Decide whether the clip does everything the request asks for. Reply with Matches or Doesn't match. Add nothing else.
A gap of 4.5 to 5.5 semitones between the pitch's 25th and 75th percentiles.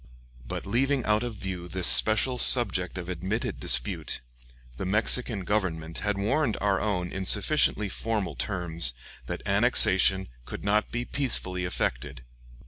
Doesn't match